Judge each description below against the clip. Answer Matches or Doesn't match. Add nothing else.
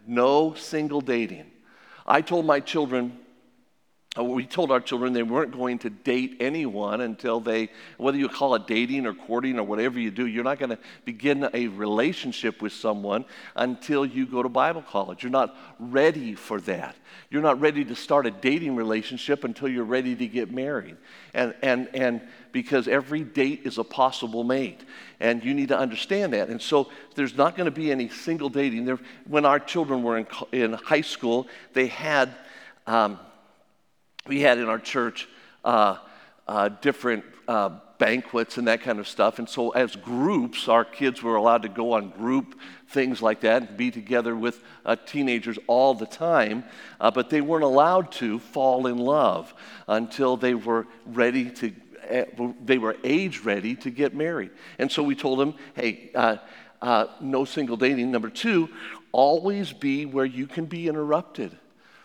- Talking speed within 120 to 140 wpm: Doesn't match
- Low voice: Matches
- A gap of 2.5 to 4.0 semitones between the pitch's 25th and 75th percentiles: Matches